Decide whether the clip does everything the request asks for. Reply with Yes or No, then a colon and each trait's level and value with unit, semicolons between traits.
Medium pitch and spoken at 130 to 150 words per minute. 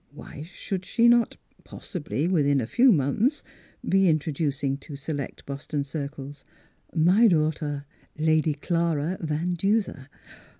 Yes: medium, 155 Hz; slow, 135 wpm